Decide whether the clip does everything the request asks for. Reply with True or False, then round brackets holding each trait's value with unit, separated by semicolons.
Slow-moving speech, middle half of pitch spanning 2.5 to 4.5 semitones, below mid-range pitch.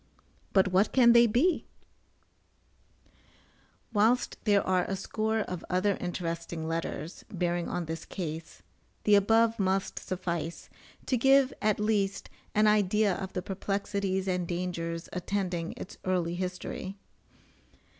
False (125 wpm; 3.1 semitones; 190 Hz)